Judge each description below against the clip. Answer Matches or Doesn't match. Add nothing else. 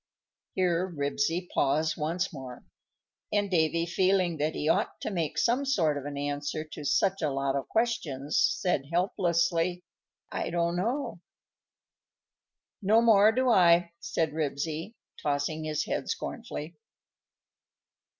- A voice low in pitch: Doesn't match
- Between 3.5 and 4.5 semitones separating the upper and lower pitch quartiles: Matches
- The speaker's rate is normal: Doesn't match